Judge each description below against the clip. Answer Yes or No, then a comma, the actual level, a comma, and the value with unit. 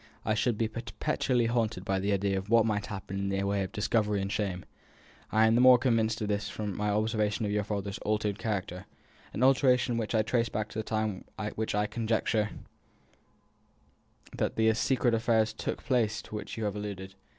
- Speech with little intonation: Yes, narrow, 2.0 semitones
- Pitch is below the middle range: Yes, low, 110 Hz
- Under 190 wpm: No, average, 195 wpm